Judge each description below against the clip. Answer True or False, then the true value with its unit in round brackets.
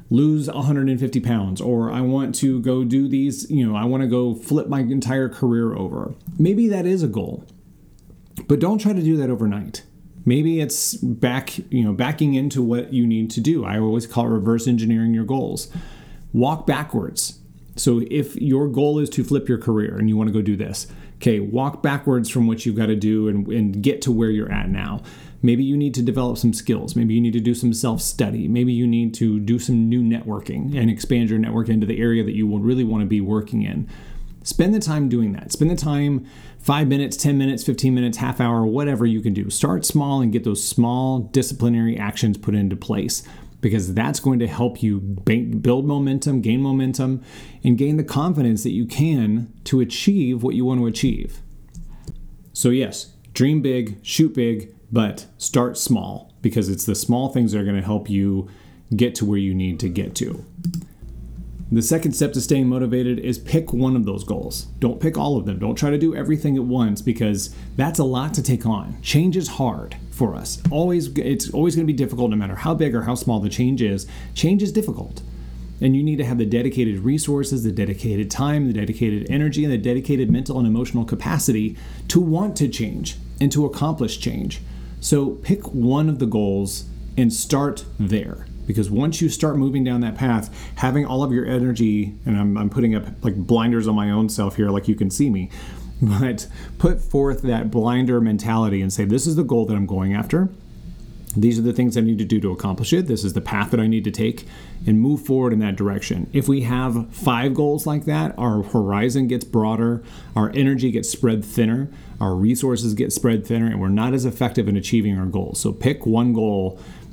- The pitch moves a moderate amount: True (4.1 semitones)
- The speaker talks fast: True (210 wpm)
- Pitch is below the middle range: True (120 Hz)